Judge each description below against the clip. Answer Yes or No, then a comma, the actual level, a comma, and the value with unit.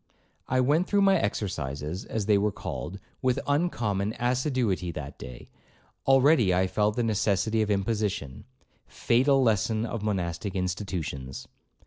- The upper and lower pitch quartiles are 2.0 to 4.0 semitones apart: No, average, 5.1 semitones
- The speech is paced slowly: Yes, slow, 125 wpm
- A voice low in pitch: Yes, low, 105 Hz